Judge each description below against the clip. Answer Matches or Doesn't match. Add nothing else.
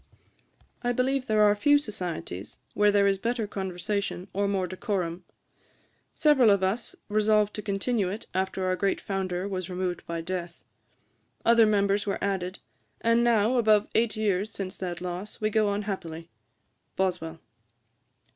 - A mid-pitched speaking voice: Doesn't match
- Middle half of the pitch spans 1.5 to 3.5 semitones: Matches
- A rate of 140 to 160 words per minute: Matches